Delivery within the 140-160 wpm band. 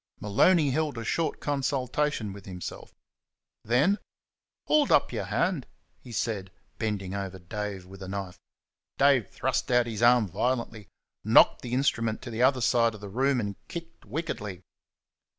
Yes: average, 150 wpm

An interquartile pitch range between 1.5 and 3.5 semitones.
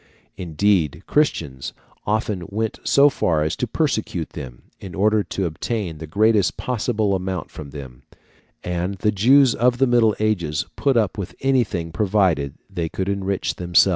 No: average, 4.7 semitones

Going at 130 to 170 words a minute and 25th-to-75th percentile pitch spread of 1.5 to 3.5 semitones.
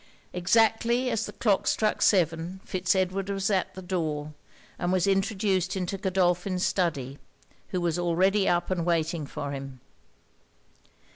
Yes: average, 140 wpm; narrow, 2.4 semitones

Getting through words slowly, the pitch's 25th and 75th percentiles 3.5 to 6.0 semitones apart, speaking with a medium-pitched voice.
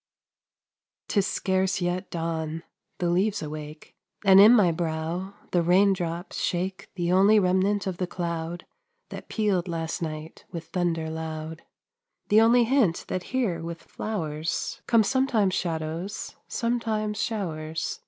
Yes: slow, 130 wpm; average, 3.8 semitones; medium, 180 Hz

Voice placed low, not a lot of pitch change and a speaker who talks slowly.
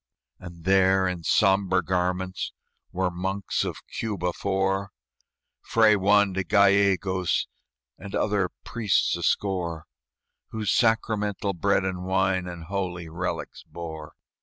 Yes: very low, 95 Hz; narrow, 1.8 semitones; slow, 115 wpm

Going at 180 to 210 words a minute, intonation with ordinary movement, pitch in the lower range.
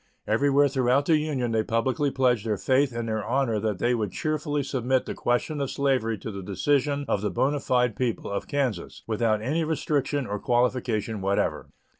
Yes: average, 185 wpm; average, 4.2 semitones; low, 125 Hz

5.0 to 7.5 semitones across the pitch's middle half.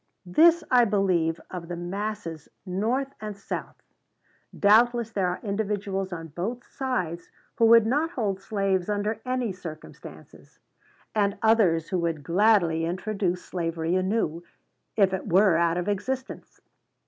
No: average, 4.0 semitones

